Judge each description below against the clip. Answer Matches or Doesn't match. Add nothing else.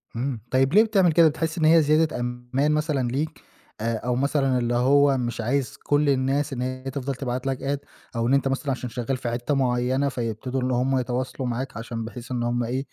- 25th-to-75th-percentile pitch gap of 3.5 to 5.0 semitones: Doesn't match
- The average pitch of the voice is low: Matches